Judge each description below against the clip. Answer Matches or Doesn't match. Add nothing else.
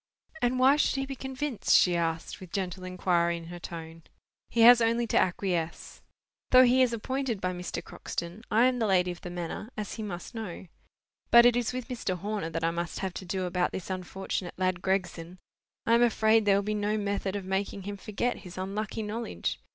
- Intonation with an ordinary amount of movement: Matches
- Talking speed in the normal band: Doesn't match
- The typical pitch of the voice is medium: Doesn't match